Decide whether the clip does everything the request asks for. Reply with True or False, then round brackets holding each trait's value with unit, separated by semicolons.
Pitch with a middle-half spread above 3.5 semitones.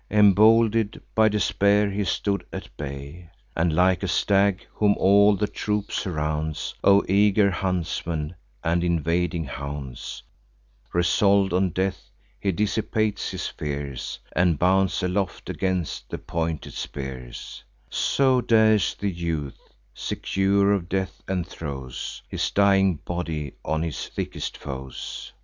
True (4.2 semitones)